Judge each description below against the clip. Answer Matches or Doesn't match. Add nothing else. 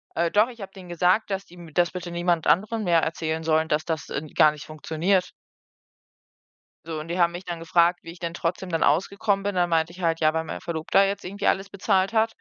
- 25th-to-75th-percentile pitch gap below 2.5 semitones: Doesn't match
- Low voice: Doesn't match